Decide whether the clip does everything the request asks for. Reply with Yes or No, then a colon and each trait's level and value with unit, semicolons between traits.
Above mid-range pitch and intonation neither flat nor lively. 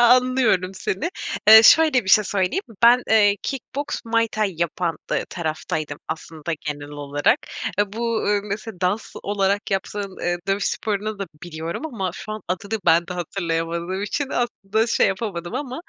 Yes: high, 200 Hz; average, 4.3 semitones